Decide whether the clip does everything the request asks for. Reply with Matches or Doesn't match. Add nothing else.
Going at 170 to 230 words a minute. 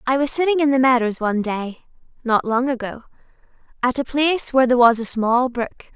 Matches